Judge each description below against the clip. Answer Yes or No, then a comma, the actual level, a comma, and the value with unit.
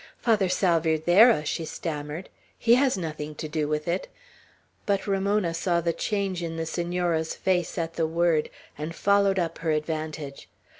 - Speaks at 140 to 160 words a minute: Yes, average, 155 wpm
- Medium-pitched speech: Yes, medium, 170 Hz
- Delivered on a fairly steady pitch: No, average, 3.3 semitones